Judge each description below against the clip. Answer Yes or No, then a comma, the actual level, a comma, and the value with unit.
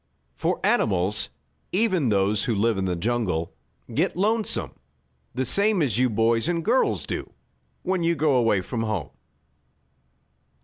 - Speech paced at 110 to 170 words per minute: Yes, average, 140 wpm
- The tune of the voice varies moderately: No, wide, 8.4 semitones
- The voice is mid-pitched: No, low, 120 Hz